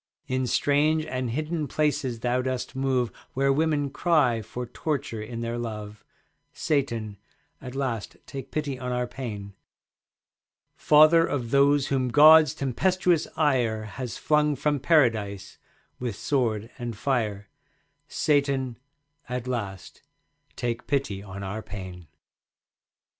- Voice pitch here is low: Yes, low, 130 Hz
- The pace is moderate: No, slow, 120 wpm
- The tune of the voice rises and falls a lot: No, average, 4.1 semitones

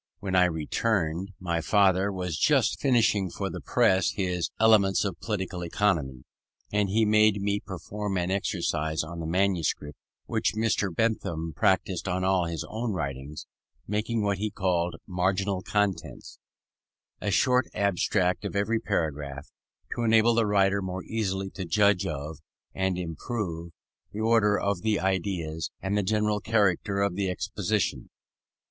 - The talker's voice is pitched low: Yes, very low, 95 Hz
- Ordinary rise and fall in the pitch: Yes, average, 3.1 semitones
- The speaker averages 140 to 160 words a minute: Yes, average, 145 wpm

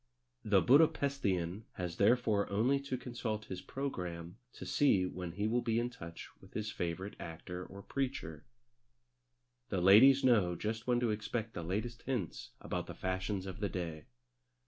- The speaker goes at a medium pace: Yes, average, 165 wpm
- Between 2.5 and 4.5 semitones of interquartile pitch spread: No, average, 5.1 semitones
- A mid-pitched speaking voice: No, low, 105 Hz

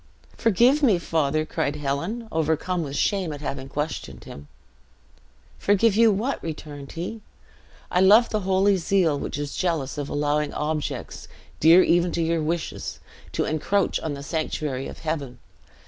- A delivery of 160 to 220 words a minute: No, average, 150 wpm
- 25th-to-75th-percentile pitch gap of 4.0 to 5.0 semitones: Yes, average, 4.6 semitones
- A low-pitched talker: No, medium, 160 Hz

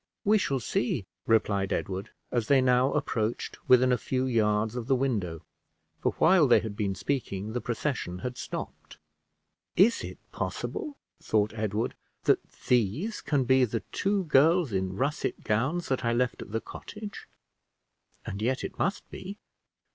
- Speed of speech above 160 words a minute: No, average, 155 wpm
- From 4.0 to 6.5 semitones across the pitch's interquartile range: Yes, average, 4.9 semitones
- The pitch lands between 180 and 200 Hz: No, low, 125 Hz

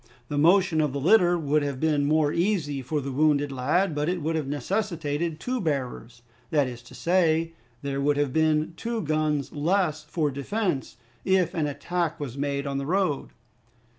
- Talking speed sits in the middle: Yes, average, 180 wpm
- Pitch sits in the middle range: Yes, medium, 155 Hz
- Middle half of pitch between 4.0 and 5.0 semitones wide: No, average, 3.3 semitones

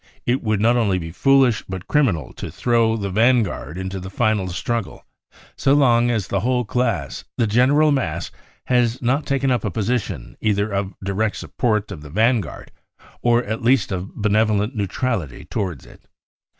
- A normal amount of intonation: Yes, average, 4.1 semitones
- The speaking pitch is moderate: No, low, 110 Hz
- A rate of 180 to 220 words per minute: No, average, 165 wpm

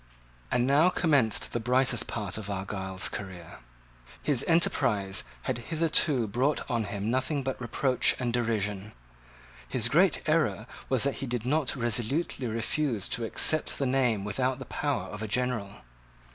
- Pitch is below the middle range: Yes, low, 120 Hz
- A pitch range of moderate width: Yes, average, 4.2 semitones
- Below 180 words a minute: Yes, average, 150 wpm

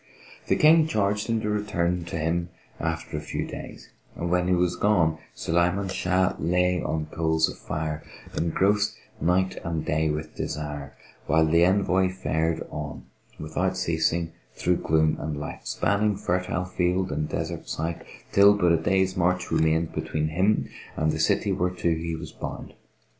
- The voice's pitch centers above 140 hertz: No, very low, 85 Hz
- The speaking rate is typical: Yes, average, 160 wpm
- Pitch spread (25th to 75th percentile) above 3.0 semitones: No, average, 2.7 semitones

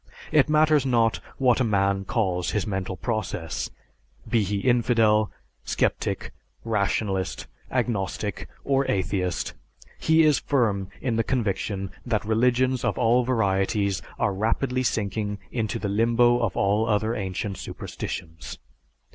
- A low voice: Yes, low, 110 Hz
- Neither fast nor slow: No, slow, 125 wpm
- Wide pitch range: No, average, 3.8 semitones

